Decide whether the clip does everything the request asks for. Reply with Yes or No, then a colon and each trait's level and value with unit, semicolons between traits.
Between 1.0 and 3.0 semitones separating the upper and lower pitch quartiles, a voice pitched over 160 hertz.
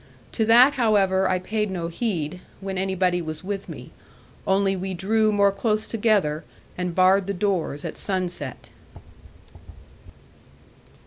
Yes: narrow, 2.5 semitones; high, 190 Hz